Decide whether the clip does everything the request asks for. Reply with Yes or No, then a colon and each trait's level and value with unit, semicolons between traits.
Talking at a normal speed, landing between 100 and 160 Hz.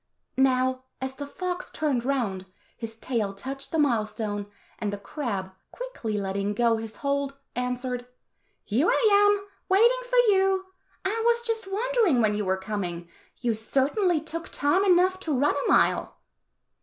No: average, 155 wpm; very high, 265 Hz